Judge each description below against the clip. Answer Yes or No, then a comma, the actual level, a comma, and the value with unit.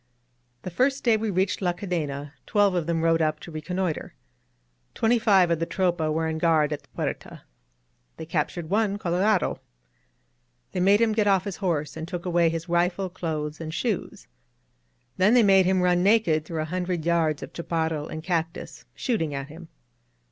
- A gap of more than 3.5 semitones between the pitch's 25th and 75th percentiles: No, average, 3.2 semitones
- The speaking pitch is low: No, medium, 175 Hz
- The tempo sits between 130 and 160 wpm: No, average, 180 wpm